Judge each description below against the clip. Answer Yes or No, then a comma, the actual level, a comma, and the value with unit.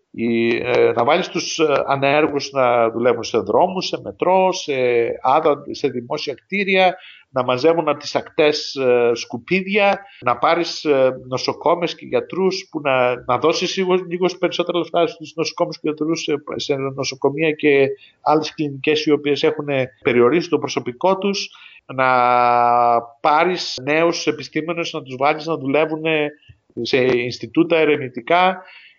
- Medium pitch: Yes, medium, 150 Hz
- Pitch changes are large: No, average, 4.6 semitones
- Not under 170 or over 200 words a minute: No, slow, 135 wpm